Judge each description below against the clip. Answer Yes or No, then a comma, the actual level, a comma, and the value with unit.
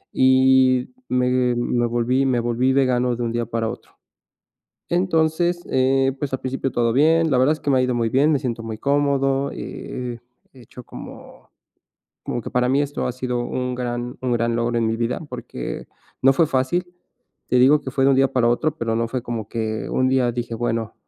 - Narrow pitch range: Yes, narrow, 2.1 semitones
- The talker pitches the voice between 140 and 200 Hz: No, low, 125 Hz